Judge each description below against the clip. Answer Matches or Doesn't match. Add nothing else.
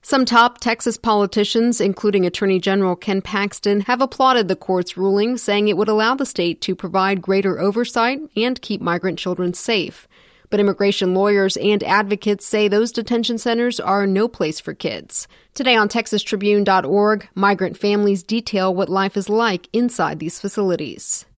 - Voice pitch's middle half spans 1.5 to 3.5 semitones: Matches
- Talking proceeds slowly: Doesn't match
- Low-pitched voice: Doesn't match